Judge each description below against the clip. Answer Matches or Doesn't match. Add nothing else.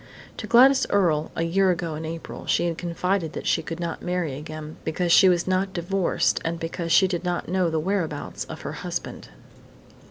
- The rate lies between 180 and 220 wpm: Matches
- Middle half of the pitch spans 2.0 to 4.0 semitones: Matches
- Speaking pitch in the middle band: Matches